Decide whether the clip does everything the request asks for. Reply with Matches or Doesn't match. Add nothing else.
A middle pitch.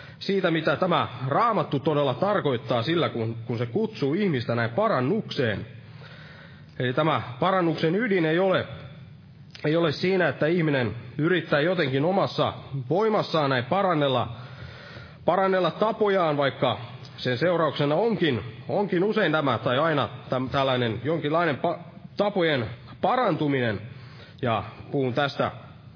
Matches